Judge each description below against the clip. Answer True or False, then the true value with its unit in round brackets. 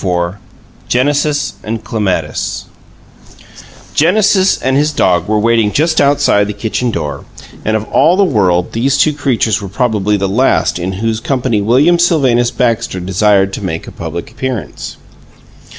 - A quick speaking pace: False (150 wpm)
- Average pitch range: False (5.8 semitones)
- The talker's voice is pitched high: False (115 Hz)